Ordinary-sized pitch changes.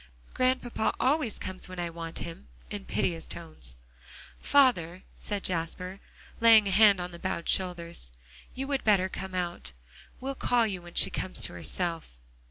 Yes: average, 4.4 semitones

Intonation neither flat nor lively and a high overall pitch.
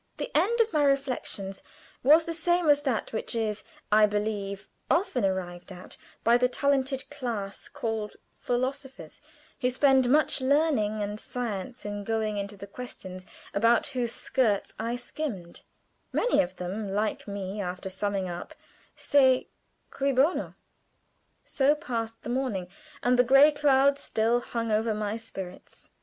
Yes: average, 4.9 semitones; high, 230 Hz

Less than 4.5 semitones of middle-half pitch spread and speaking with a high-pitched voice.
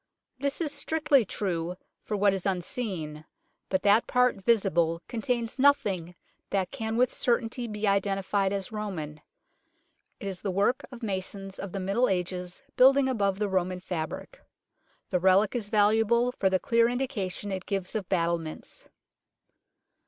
Yes: average, 4.0 semitones; high, 200 Hz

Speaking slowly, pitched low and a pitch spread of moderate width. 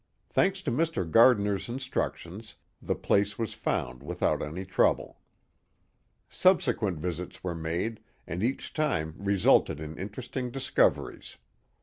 No: slow, 115 wpm; low, 100 Hz; wide, 6.5 semitones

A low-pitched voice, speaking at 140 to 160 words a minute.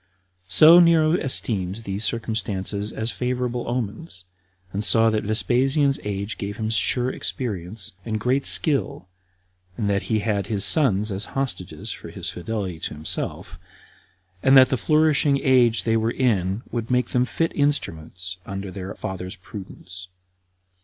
Yes: low, 110 Hz; average, 145 wpm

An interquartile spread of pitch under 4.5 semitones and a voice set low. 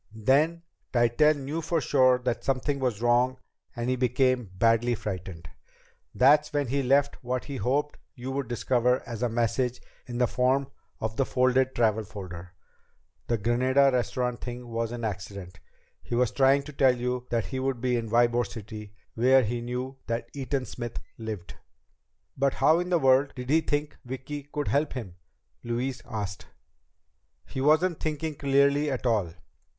Yes: average, 2.8 semitones; low, 125 Hz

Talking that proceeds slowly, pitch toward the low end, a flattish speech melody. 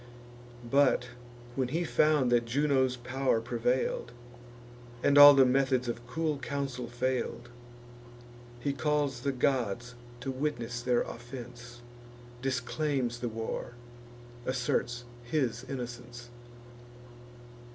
Yes: slow, 100 wpm; low, 125 Hz; narrow, 2.2 semitones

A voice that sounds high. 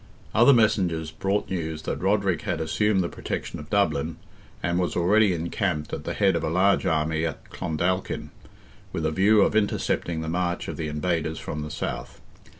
No: very low, 85 Hz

